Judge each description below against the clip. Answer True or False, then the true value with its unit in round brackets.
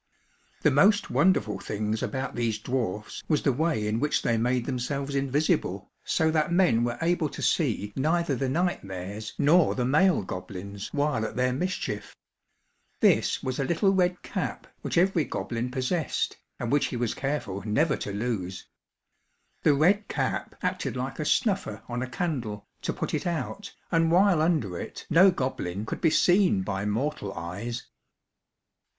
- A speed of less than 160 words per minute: False (165 wpm)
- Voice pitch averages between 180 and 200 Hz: False (130 Hz)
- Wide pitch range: True (7.2 semitones)